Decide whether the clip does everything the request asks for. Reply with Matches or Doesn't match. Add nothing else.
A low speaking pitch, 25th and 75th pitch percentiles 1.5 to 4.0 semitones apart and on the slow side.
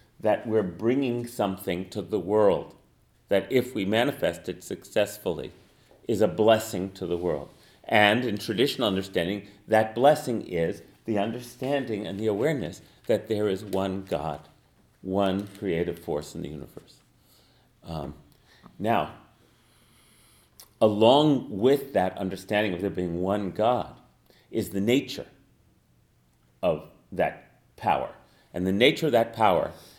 Matches